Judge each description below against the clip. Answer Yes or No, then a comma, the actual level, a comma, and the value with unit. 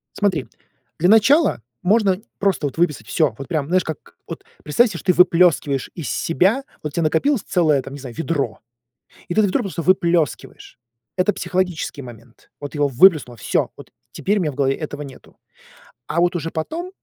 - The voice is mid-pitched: Yes, medium, 165 Hz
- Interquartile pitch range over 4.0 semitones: Yes, average, 4.6 semitones